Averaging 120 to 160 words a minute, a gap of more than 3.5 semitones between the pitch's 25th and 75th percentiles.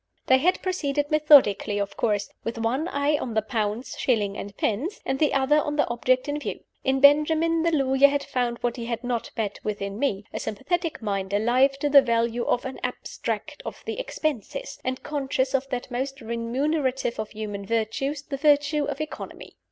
No: average, 190 wpm; average, 4.2 semitones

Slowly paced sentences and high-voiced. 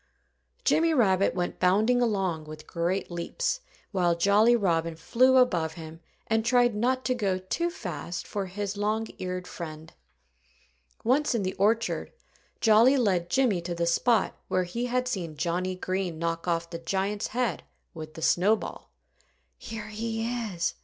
No: average, 155 wpm; high, 195 Hz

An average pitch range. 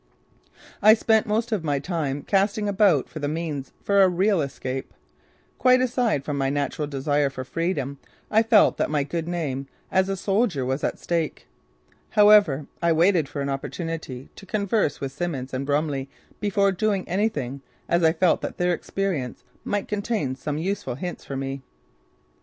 No: wide, 6.2 semitones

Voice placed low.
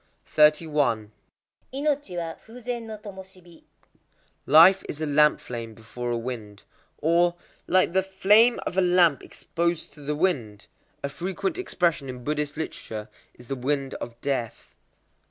No: medium, 155 Hz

